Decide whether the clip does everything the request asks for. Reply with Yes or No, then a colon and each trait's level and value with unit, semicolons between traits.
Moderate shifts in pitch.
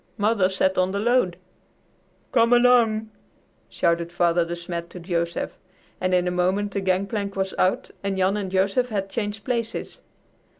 Yes: average, 3.0 semitones